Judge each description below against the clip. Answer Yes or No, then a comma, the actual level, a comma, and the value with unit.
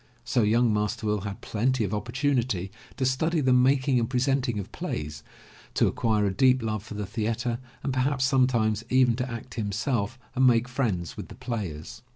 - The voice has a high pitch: No, low, 120 Hz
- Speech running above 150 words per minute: Yes, average, 185 wpm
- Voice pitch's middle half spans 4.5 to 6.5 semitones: No, average, 3.5 semitones